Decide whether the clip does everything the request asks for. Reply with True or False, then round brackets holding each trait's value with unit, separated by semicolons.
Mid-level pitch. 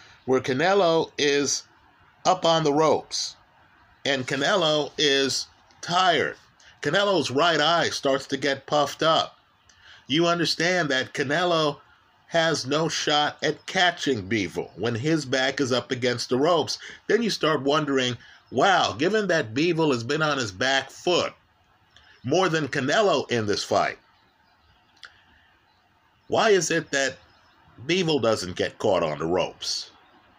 True (145 Hz)